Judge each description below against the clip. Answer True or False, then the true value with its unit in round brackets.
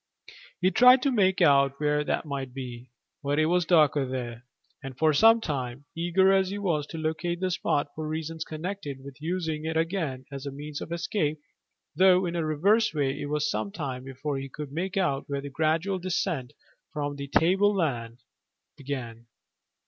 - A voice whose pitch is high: False (150 Hz)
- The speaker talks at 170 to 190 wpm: True (180 wpm)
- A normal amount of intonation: True (4.3 semitones)